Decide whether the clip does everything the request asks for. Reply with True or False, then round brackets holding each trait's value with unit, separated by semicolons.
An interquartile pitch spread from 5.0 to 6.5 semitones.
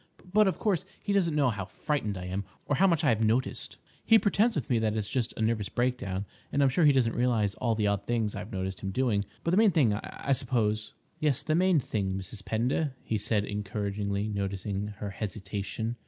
True (5.5 semitones)